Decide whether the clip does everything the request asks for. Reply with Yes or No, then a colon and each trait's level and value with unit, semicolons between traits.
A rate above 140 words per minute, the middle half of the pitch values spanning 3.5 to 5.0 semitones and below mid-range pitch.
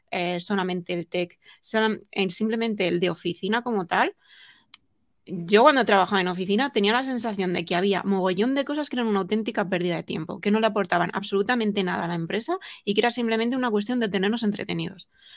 No: fast, 190 wpm; average, 4.0 semitones; high, 205 Hz